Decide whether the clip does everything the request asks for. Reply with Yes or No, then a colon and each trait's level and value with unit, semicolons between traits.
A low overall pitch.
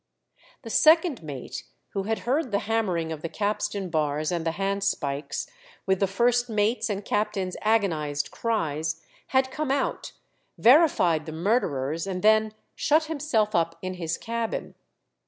No: high, 200 Hz